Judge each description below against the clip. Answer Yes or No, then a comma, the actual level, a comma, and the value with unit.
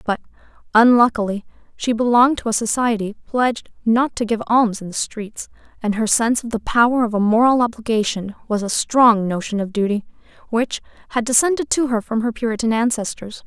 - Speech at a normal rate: Yes, average, 180 wpm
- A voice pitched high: Yes, high, 230 Hz